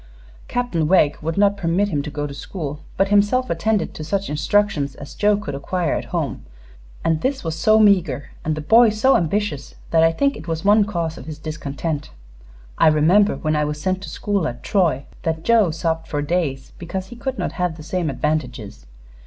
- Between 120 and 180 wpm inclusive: No, average, 200 wpm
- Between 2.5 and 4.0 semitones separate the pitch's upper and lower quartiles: No, average, 5.2 semitones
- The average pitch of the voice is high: No, medium, 165 Hz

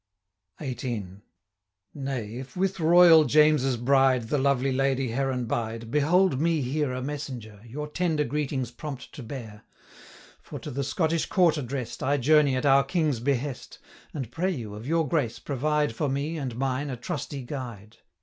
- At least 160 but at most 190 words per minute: Yes, average, 165 wpm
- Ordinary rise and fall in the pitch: Yes, average, 3.4 semitones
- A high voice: No, low, 135 Hz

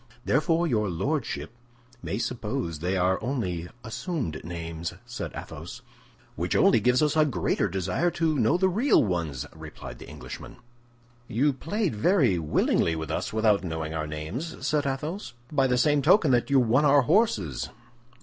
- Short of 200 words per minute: Yes, average, 160 wpm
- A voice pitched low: Yes, low, 120 Hz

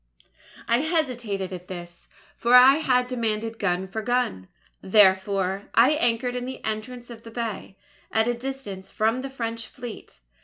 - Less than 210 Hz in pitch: No, high, 230 Hz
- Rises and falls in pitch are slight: No, average, 4.1 semitones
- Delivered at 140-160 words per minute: Yes, average, 155 wpm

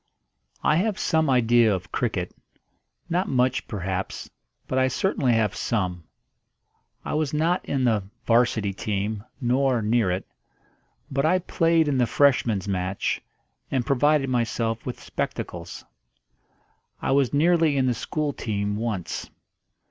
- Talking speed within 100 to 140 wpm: Yes, slow, 135 wpm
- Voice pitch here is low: Yes, low, 125 Hz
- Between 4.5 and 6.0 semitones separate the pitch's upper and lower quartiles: Yes, average, 5.2 semitones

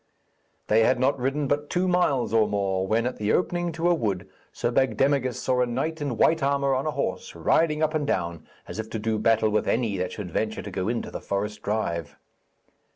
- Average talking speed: No, fast, 220 wpm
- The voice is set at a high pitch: No, low, 120 Hz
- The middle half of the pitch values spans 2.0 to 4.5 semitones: No, average, 5.3 semitones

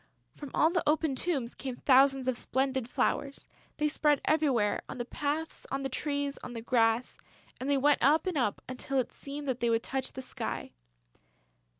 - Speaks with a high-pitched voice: Yes, very high, 270 Hz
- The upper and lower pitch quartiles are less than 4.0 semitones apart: Yes, average, 2.7 semitones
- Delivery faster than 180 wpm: Yes, average, 190 wpm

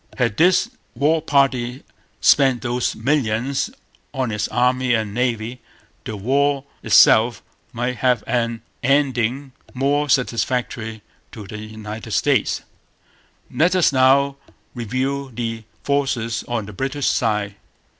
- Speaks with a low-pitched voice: Yes, low, 125 Hz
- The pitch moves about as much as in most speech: Yes, average, 3.4 semitones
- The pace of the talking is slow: Yes, slow, 120 wpm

